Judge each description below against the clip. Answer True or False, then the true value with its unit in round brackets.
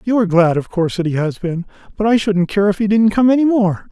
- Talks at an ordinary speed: False (290 wpm)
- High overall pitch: True (200 Hz)